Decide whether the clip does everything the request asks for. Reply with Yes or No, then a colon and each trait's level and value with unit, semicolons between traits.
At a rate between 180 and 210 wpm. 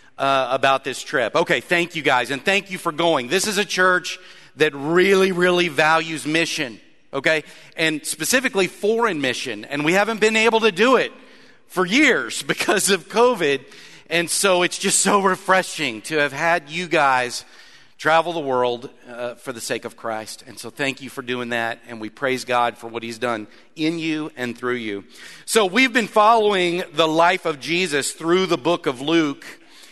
Yes: average, 185 wpm